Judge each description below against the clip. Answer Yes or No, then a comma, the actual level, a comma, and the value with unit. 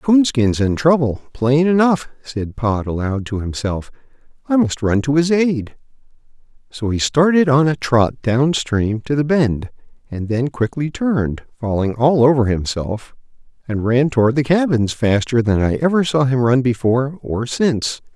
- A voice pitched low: Yes, low, 130 Hz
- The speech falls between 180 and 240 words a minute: No, average, 165 wpm